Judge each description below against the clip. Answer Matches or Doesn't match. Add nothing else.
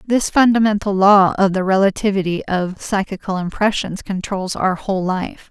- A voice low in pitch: Doesn't match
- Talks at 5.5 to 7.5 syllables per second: Doesn't match